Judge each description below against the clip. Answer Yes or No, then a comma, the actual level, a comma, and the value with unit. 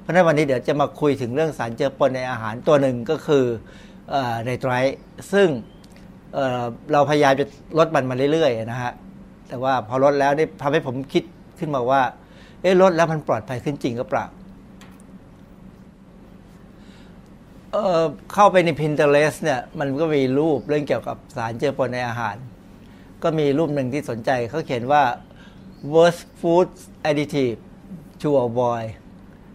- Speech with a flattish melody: No, average, 4.0 semitones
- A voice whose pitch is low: No, medium, 145 Hz